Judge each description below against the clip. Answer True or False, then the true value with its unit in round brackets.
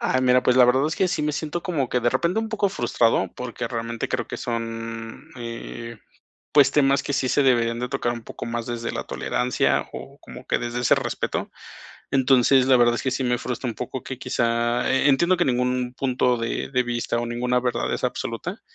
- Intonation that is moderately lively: False (2.1 semitones)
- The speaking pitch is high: False (125 Hz)